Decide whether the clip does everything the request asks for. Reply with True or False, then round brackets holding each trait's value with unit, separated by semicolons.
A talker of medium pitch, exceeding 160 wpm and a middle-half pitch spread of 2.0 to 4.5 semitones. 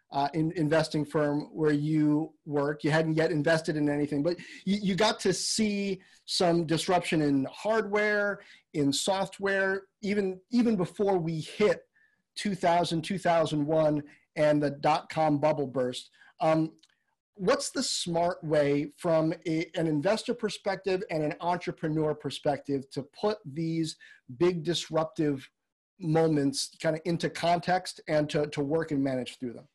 False (160 Hz; 140 wpm; 4.0 semitones)